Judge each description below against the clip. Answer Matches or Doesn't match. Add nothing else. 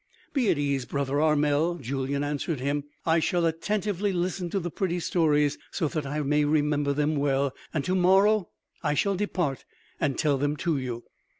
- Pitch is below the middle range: Doesn't match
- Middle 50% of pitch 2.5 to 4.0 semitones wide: Matches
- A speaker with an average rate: Matches